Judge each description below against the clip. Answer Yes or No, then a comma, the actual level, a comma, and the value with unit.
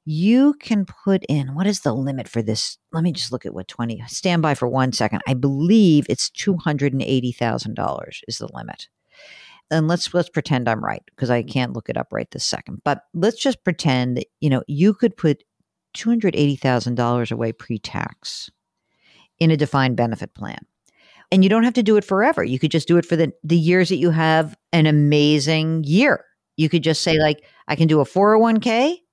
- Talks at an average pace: Yes, average, 195 wpm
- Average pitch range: No, wide, 6.0 semitones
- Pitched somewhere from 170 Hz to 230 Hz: No, medium, 155 Hz